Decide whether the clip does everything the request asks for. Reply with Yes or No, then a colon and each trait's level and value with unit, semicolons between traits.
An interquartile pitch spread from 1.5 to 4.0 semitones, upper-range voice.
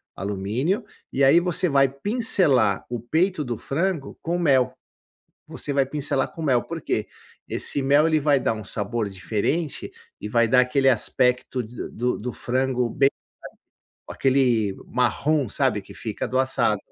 No: average, 3.6 semitones; low, 130 Hz